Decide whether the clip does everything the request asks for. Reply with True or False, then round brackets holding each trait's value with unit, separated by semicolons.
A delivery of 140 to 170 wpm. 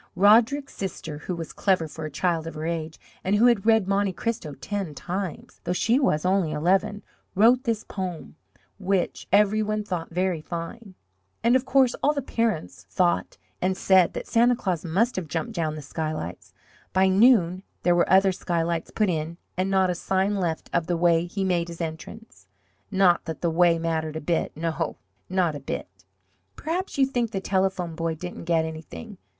False (185 wpm)